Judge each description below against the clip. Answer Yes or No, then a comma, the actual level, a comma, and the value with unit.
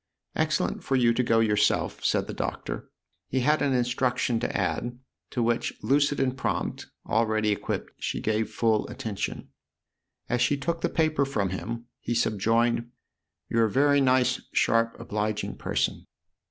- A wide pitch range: No, average, 3.0 semitones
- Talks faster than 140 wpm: Yes, average, 160 wpm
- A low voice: Yes, low, 120 Hz